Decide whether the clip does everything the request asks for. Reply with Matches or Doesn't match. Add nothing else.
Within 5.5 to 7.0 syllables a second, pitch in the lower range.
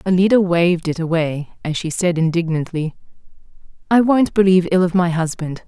Doesn't match